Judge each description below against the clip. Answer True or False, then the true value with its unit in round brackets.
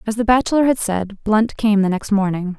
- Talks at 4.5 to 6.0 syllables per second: True (5.4 syllables/s)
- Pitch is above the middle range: True (210 Hz)